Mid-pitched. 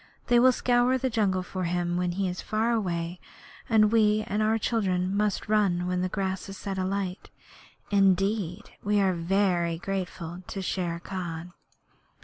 No: high, 195 Hz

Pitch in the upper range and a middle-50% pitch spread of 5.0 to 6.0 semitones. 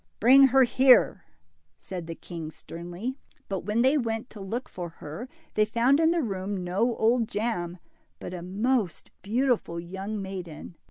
Yes: high, 205 Hz; wide, 5.6 semitones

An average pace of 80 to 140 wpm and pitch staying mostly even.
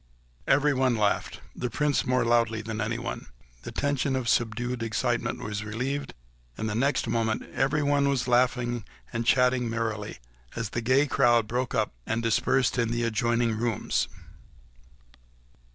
Yes: slow, 135 wpm; narrow, 2.3 semitones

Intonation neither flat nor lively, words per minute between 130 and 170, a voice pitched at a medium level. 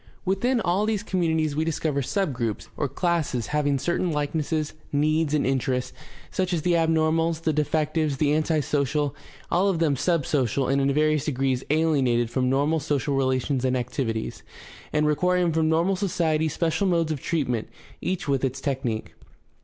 Yes: average, 3.3 semitones; average, 165 wpm; medium, 150 Hz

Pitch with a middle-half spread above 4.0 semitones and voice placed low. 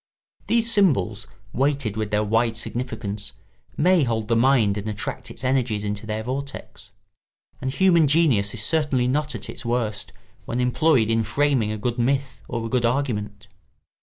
Yes: average, 4.4 semitones; low, 120 Hz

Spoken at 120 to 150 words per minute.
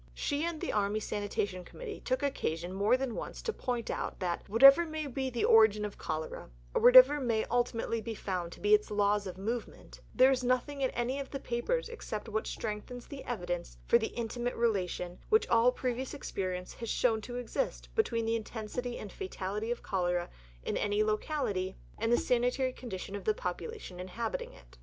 No: average, 190 wpm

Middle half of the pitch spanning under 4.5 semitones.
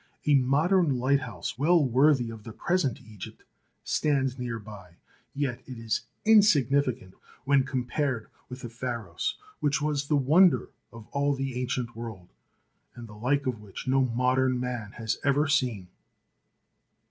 Yes: average, 3.5 semitones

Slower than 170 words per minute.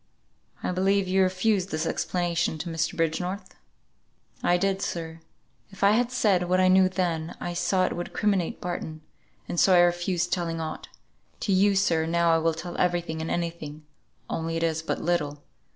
No: average, 185 wpm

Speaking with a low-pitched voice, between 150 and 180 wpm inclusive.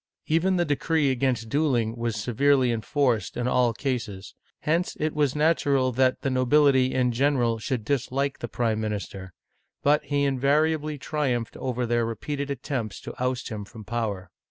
Yes: low, 130 Hz; average, 160 wpm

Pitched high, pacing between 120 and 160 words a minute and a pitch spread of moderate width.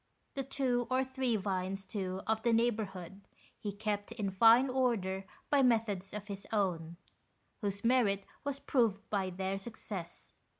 Yes: high, 210 Hz; average, 145 wpm; average, 3.8 semitones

